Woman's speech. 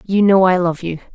Yes: female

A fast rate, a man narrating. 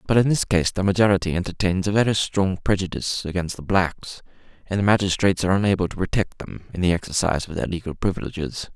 No: average, 190 wpm; male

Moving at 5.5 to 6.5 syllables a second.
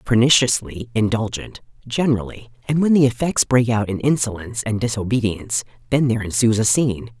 Yes: 5.9 syllables/s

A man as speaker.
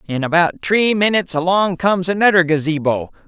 Yes: male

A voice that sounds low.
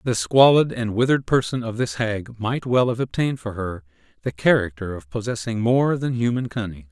Yes: low, 115 Hz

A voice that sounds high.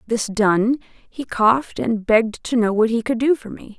Yes: high, 230 Hz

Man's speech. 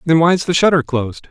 Yes: male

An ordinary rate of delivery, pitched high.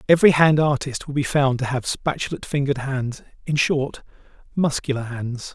No: average, 150 wpm; low, 135 Hz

